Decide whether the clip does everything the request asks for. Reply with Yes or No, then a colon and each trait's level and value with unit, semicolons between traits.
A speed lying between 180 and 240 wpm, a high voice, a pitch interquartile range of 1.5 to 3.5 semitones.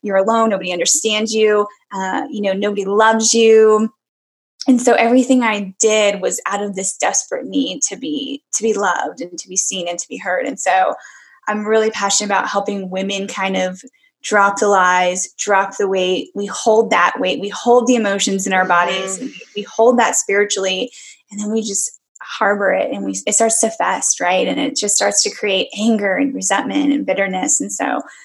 Yes: average, 200 wpm; high, 205 Hz; average, 2.8 semitones